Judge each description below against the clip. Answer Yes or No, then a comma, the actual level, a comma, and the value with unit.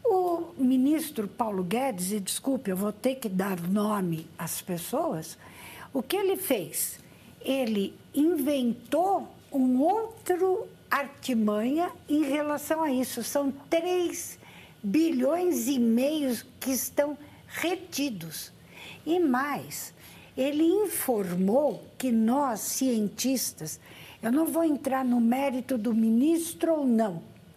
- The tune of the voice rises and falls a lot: Yes, wide, 5.9 semitones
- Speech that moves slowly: Yes, slow, 115 wpm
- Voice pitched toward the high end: Yes, very high, 265 Hz